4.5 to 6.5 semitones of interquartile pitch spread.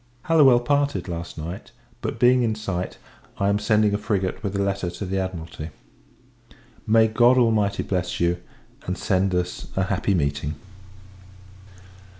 No: average, 3.6 semitones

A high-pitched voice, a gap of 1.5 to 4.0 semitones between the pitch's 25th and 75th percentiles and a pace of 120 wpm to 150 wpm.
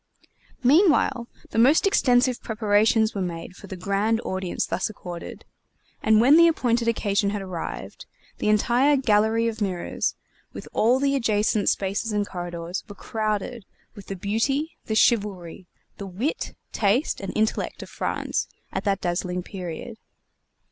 Yes: high, 215 Hz; average, 3.6 semitones; average, 145 wpm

